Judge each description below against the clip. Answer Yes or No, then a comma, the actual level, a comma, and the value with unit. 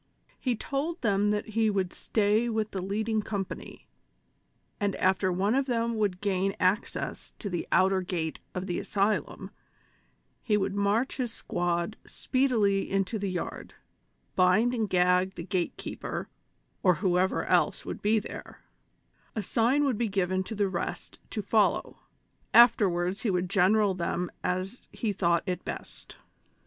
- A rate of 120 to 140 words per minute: No, average, 155 wpm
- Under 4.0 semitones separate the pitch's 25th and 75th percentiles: Yes, average, 3.2 semitones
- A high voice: Yes, high, 200 Hz